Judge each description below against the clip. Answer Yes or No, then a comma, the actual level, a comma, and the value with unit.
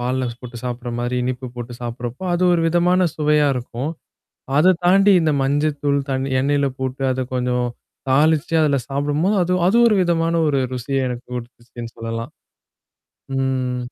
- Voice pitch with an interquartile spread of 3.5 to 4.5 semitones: Yes, average, 3.8 semitones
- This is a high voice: No, low, 135 Hz